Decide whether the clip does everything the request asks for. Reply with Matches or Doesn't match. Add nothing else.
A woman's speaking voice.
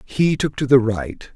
Doesn't match